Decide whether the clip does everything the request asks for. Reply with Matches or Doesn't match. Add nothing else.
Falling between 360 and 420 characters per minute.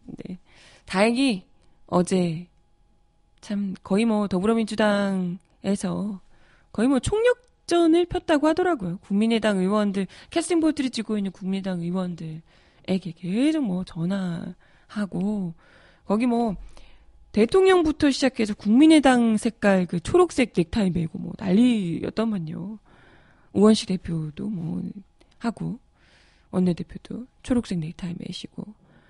Doesn't match